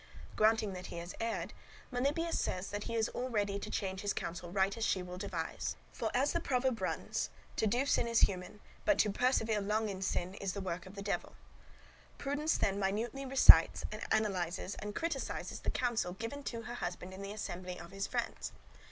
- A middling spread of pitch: Yes, average, 4.1 semitones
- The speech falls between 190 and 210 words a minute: Yes, average, 195 wpm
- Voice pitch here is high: Yes, high, 205 Hz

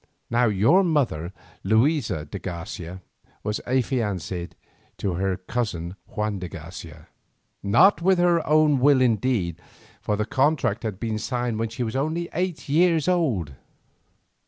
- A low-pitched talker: Yes, low, 115 Hz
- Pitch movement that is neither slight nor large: No, wide, 7.6 semitones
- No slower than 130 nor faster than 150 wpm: Yes, slow, 135 wpm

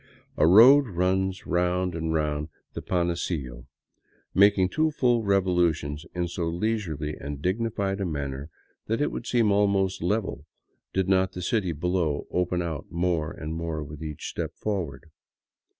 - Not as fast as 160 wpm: Yes, average, 150 wpm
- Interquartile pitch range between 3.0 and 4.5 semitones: Yes, average, 3.8 semitones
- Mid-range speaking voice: No, very low, 90 Hz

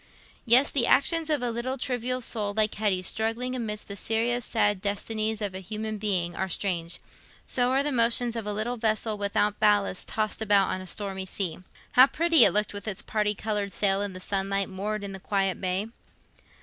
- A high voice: Yes, high, 210 Hz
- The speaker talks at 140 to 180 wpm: No, average, 200 wpm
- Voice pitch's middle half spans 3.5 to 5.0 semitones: No, average, 2.9 semitones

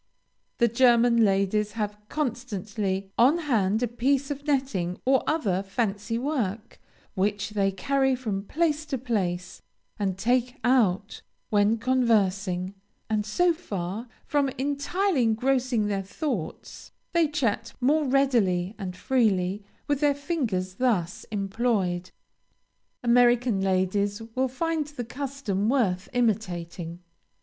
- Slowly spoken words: Yes, slow, 120 wpm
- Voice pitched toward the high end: Yes, high, 230 Hz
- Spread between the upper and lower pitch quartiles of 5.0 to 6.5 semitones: Yes, average, 5.3 semitones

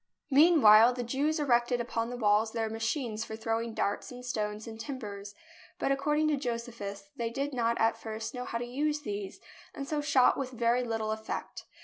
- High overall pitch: Yes, high, 235 Hz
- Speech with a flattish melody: No, average, 3.4 semitones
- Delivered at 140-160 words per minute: No, average, 195 wpm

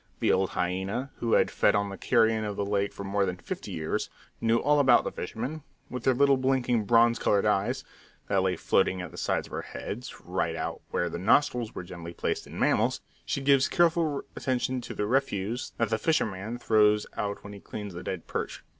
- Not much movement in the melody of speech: No, average, 4.5 semitones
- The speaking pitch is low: Yes, low, 110 Hz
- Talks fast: Yes, fast, 210 wpm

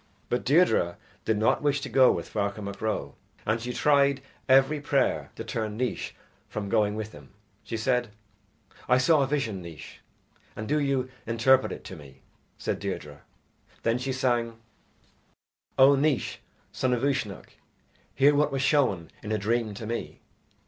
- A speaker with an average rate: Yes, average, 165 wpm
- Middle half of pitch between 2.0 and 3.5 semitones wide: No, average, 4.1 semitones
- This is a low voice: Yes, low, 120 Hz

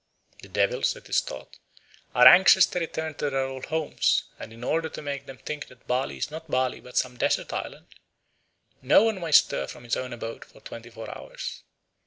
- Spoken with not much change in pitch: No, average, 4.4 semitones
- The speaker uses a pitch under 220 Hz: Yes, low, 135 Hz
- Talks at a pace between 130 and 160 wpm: No, fast, 205 wpm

